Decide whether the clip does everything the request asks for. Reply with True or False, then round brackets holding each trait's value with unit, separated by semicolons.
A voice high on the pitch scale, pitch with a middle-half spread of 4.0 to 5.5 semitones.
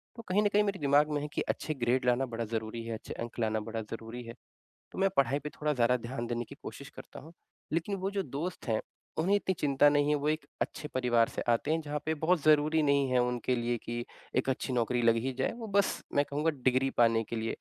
False (135 Hz; 4.4 semitones)